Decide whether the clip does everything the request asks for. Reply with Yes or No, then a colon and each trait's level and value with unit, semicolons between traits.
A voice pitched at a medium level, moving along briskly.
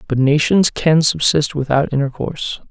No: medium, 150 Hz; slow, 135 wpm